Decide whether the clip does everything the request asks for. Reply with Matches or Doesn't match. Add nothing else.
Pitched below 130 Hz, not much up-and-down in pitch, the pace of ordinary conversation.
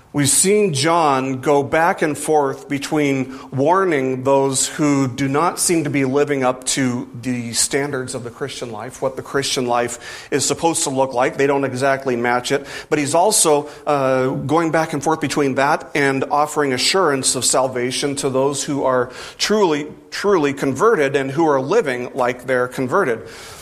Doesn't match